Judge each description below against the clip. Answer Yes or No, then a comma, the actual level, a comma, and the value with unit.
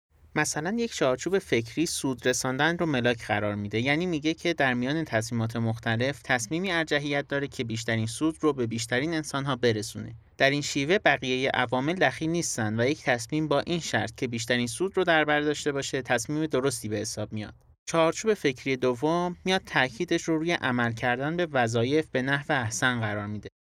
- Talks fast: Yes, fast, 185 wpm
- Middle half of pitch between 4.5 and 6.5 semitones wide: Yes, average, 5.2 semitones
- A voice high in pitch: No, low, 135 Hz